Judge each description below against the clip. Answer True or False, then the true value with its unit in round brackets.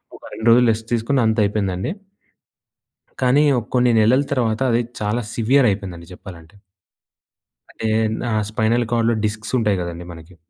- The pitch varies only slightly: False (3.5 semitones)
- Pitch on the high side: False (110 Hz)